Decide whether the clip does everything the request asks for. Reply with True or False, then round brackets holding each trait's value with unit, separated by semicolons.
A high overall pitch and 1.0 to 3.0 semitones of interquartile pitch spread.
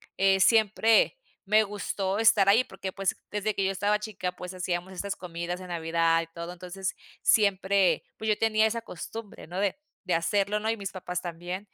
True (195 Hz; 2.7 semitones)